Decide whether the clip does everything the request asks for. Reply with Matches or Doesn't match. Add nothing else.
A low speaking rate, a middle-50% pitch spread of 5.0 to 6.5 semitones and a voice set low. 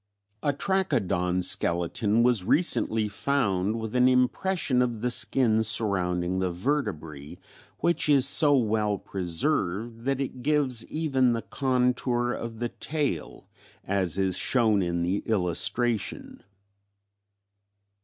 Matches